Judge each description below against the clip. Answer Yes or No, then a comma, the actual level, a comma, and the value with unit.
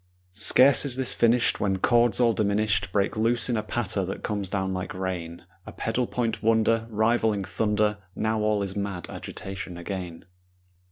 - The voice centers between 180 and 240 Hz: No, low, 105 Hz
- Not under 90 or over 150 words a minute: No, average, 165 wpm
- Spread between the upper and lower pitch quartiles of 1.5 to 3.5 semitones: Yes, average, 2.9 semitones